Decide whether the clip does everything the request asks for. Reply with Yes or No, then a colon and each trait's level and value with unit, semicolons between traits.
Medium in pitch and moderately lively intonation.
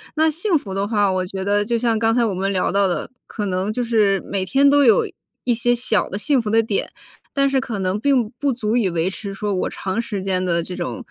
No: high, 210 Hz; average, 3.9 semitones